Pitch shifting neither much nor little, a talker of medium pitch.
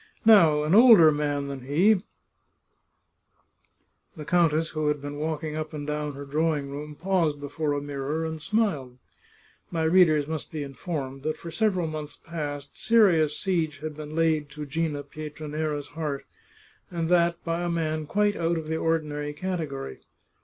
No: narrow, 2.2 semitones; medium, 155 Hz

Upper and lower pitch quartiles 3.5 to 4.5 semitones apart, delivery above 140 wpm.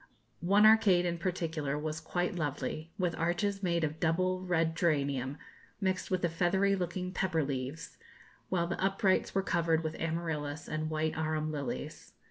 No: average, 2.8 semitones; average, 155 wpm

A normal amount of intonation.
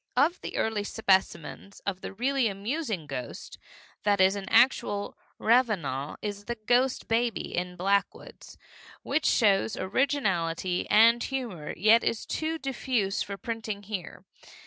Yes: average, 4.0 semitones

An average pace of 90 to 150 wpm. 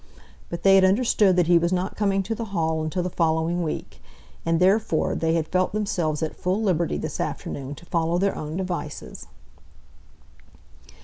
No: average, 175 wpm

